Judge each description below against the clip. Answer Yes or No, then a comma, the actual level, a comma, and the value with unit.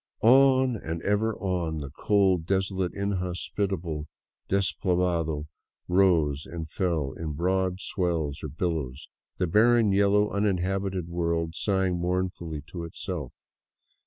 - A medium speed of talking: No, slow, 110 wpm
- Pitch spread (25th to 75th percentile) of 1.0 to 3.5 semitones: Yes, average, 3.0 semitones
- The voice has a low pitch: Yes, very low, 90 Hz